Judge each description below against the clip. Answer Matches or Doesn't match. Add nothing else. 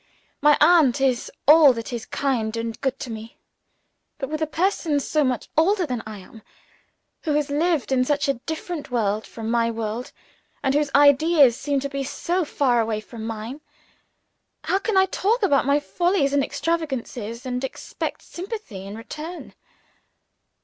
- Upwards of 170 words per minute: Doesn't match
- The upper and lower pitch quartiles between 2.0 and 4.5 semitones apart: Doesn't match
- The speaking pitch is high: Matches